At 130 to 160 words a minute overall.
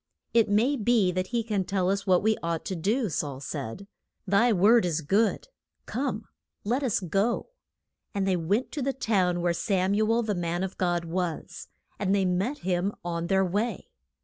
No: average, 190 wpm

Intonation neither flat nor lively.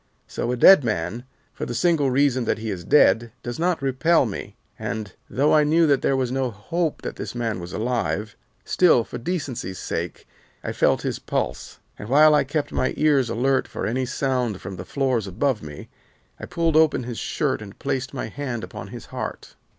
Yes: average, 4.3 semitones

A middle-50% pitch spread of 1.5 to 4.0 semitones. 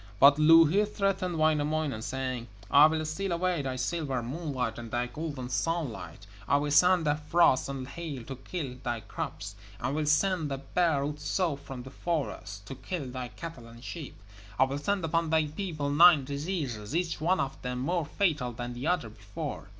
No: average, 4.5 semitones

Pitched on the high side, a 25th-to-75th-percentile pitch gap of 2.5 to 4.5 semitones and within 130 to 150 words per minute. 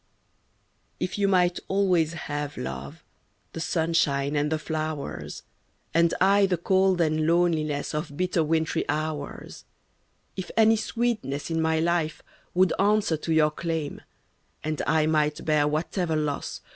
No: medium, 160 Hz; average, 2.8 semitones; average, 140 wpm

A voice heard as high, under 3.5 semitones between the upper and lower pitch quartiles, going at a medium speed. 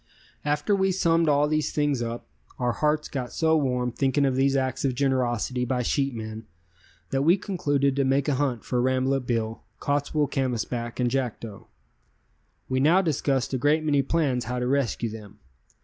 No: low, 135 Hz; average, 2.9 semitones; average, 175 wpm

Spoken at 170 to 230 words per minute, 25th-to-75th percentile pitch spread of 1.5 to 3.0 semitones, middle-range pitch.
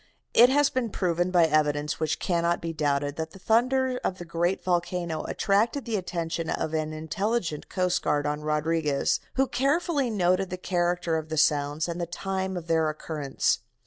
No: average, 175 wpm; average, 3.6 semitones; medium, 170 Hz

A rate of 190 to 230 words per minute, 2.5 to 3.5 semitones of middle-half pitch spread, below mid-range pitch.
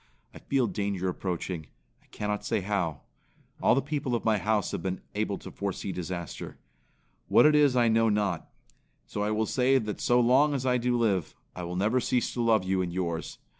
No: fast, 205 wpm; average, 4.7 semitones; low, 105 Hz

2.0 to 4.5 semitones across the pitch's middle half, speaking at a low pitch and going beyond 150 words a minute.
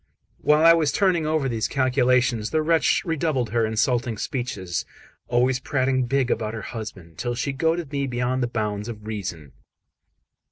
Yes: average, 4.1 semitones; low, 125 Hz; average, 160 wpm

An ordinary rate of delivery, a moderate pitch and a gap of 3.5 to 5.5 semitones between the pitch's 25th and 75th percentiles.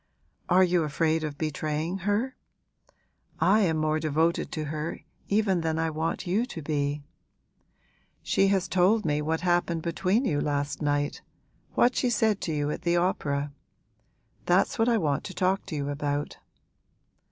Yes: average, 160 wpm; medium, 165 Hz; average, 3.9 semitones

